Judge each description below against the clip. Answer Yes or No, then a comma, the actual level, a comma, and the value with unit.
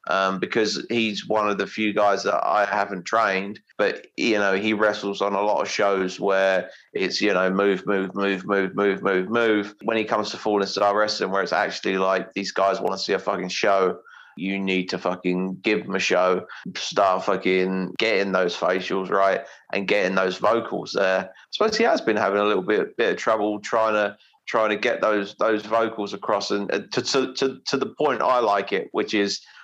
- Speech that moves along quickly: Yes, fast, 210 wpm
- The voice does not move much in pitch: Yes, narrow, 1.8 semitones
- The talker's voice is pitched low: Yes, low, 100 Hz